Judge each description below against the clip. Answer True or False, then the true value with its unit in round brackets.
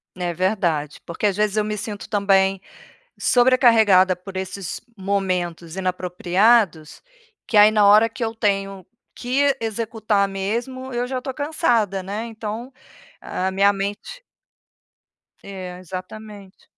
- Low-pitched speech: False (200 Hz)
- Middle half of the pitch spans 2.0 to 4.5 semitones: True (3.2 semitones)